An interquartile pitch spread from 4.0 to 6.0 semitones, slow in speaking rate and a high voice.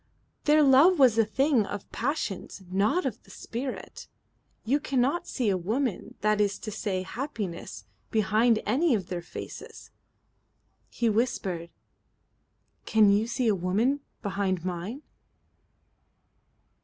Yes: average, 5.1 semitones; slow, 130 wpm; high, 220 Hz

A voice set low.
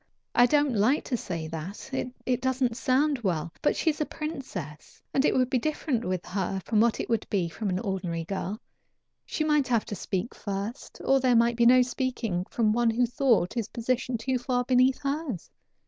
No: high, 235 Hz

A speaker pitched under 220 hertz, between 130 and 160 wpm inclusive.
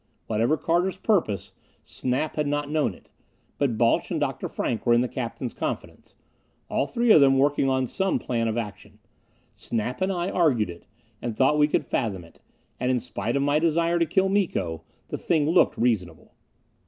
No: low, 135 Hz; average, 185 wpm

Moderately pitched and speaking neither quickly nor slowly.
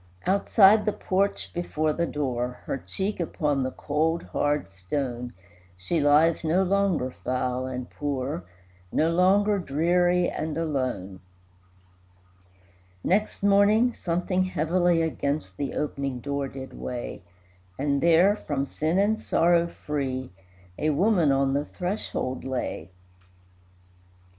No: medium, 155 Hz; slow, 120 wpm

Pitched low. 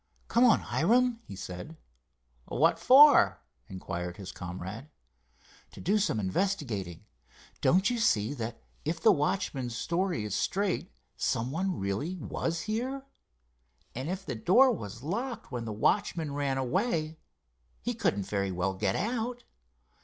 No: medium, 160 Hz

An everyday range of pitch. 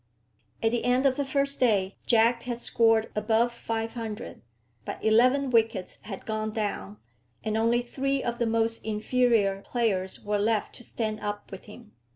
No: narrow, 2.2 semitones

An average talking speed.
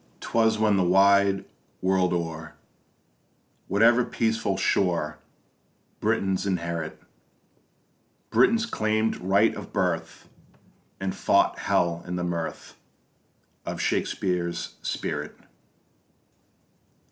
No: slow, 90 wpm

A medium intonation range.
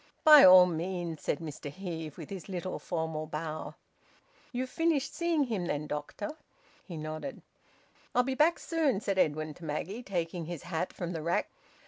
No: wide, 5.8 semitones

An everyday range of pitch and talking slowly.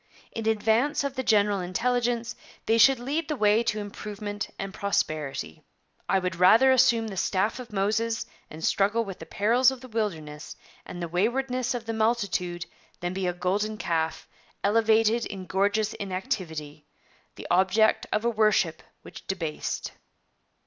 No: average, 3.9 semitones; average, 155 wpm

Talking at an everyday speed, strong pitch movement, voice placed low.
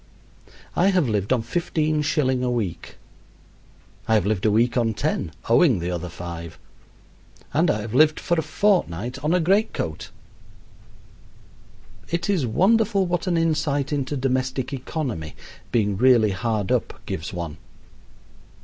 Yes: average, 145 wpm; wide, 7.2 semitones; low, 130 Hz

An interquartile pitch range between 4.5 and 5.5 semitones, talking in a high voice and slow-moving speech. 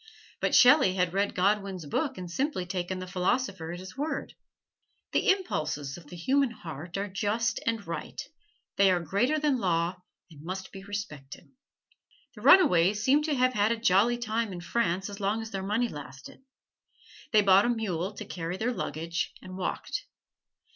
No: average, 4.8 semitones; high, 195 Hz; average, 175 wpm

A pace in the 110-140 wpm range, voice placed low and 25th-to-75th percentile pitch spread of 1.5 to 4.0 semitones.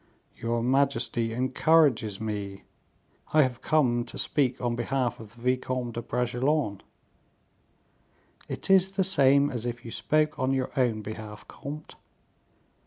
Yes: slow, 135 wpm; low, 125 Hz; average, 3.3 semitones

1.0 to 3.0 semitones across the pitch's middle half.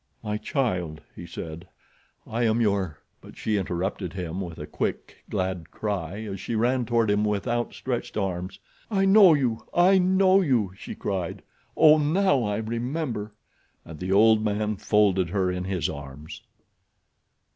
No: average, 4.7 semitones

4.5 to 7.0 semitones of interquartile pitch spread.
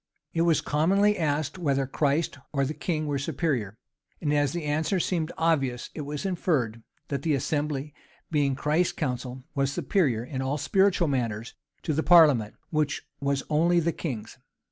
No: average, 3.4 semitones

